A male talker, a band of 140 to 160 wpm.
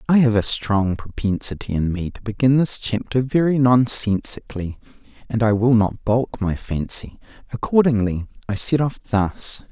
Yes: male; average, 150 wpm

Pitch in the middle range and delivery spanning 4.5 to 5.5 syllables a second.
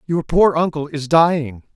Yes: medium, 155 Hz; 4.6 syllables/s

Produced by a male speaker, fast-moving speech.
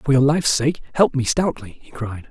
Yes: male; fast, 235 wpm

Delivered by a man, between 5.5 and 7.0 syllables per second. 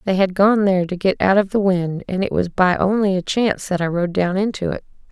No: female; 5.7 syllables/s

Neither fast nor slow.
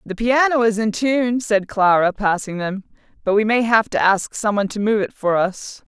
No: fast, 220 wpm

